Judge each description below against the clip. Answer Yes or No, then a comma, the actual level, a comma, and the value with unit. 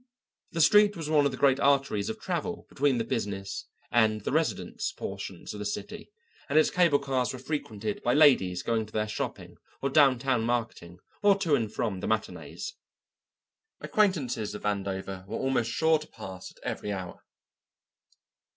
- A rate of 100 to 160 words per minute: No, average, 170 wpm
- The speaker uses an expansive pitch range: Yes, wide, 6.2 semitones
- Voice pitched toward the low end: Yes, low, 125 Hz